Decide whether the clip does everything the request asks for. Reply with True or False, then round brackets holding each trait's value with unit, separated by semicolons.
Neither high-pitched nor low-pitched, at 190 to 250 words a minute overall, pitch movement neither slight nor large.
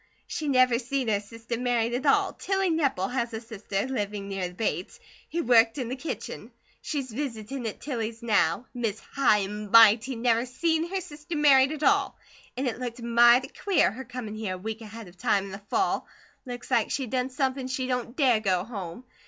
False (240 Hz; 200 wpm; 3.5 semitones)